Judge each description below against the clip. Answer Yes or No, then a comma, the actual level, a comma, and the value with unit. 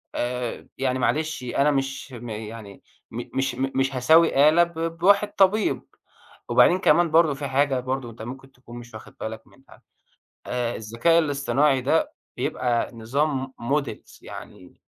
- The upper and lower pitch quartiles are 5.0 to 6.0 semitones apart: No, average, 3.8 semitones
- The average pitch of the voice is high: No, low, 135 Hz